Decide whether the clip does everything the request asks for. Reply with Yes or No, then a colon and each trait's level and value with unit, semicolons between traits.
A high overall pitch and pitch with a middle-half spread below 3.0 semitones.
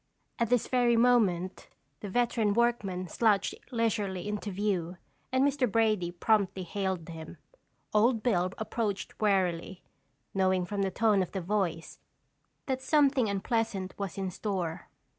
No: high, 205 Hz; average, 3.7 semitones